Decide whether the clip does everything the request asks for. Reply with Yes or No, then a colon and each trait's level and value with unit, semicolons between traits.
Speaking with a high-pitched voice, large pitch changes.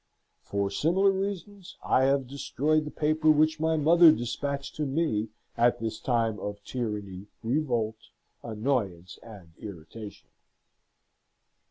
No: low, 125 Hz; wide, 6.5 semitones